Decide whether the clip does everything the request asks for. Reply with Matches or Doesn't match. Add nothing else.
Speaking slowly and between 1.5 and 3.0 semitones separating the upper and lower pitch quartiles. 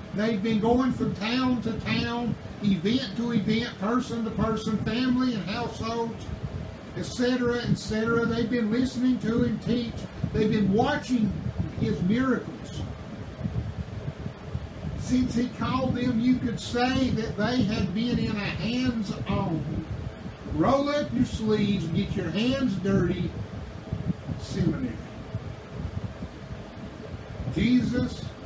Matches